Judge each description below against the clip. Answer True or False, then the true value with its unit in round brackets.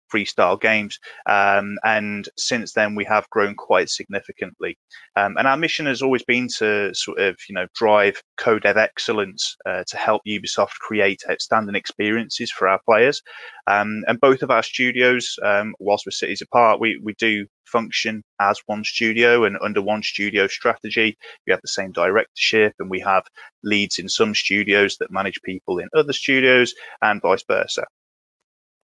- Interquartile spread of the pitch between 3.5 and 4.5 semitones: False (2.6 semitones)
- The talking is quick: False (170 wpm)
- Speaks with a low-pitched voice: True (105 Hz)